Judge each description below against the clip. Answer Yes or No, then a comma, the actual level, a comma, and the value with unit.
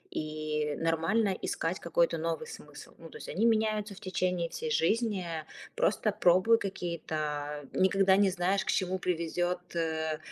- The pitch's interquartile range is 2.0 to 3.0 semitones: No, average, 3.6 semitones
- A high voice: No, medium, 180 Hz